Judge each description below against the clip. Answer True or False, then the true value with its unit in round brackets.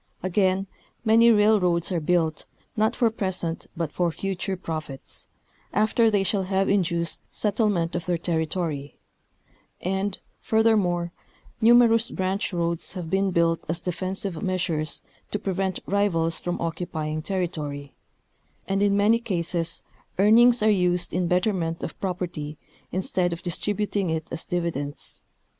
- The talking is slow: True (130 wpm)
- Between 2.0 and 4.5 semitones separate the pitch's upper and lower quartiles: True (3.2 semitones)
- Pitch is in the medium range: True (180 Hz)